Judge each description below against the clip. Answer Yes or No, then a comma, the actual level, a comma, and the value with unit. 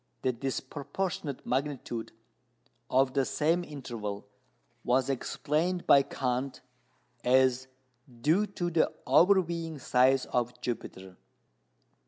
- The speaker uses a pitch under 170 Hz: Yes, low, 135 Hz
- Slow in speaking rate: Yes, slow, 95 wpm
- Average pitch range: Yes, average, 4.3 semitones